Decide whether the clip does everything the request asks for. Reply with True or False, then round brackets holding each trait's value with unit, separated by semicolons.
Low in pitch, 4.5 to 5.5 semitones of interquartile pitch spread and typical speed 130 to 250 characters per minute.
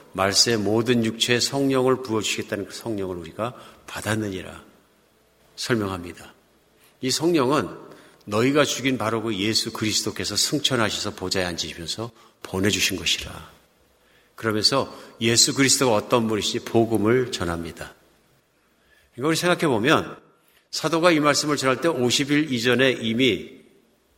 False (115 Hz; 5.1 semitones; 295 characters per minute)